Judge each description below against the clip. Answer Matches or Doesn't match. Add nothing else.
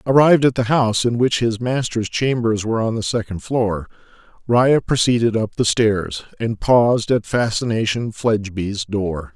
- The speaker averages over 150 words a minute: Matches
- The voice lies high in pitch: Doesn't match